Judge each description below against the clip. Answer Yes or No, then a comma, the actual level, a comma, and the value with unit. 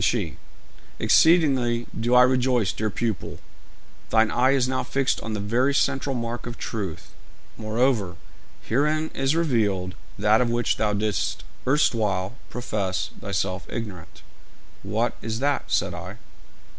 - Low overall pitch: Yes, low, 115 Hz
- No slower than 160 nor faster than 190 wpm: No, slow, 135 wpm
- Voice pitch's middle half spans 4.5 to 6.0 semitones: No, average, 3.7 semitones